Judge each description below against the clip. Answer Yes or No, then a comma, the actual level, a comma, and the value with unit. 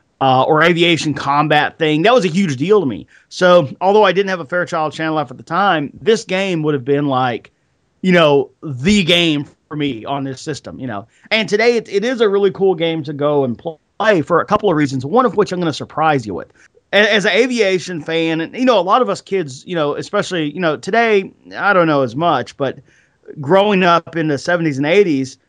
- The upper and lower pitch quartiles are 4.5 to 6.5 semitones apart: Yes, average, 4.8 semitones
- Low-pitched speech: No, medium, 165 Hz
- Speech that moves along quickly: Yes, fast, 235 wpm